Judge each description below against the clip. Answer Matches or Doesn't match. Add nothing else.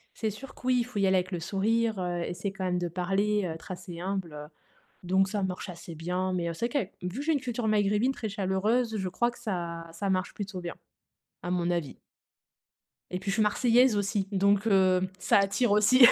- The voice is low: Doesn't match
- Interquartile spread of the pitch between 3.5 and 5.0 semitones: Doesn't match